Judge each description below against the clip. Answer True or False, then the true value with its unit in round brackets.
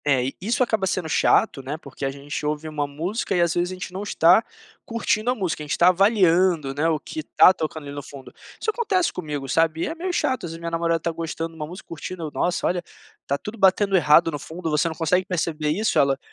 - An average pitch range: True (3.8 semitones)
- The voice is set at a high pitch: False (165 Hz)